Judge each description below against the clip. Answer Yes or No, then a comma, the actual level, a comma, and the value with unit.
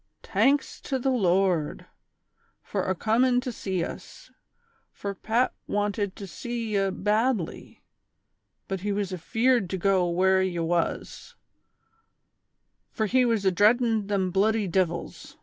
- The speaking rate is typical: No, slow, 125 wpm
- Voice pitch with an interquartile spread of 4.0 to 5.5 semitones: No, average, 3.3 semitones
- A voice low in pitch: No, high, 200 Hz